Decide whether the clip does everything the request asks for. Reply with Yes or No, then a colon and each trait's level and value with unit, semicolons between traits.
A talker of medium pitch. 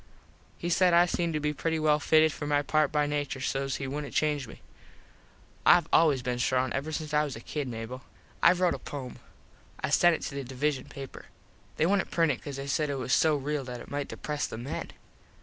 Yes: medium, 145 Hz